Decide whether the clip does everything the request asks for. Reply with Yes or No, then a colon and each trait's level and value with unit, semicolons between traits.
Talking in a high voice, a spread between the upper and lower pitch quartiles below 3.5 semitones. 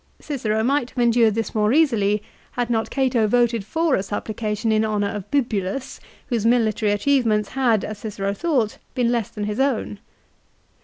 Yes: high, 225 Hz; average, 2.9 semitones